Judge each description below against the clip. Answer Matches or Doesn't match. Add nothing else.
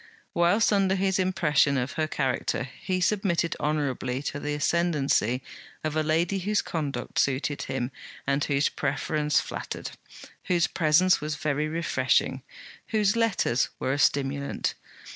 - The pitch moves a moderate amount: Matches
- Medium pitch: Matches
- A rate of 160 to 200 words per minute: Doesn't match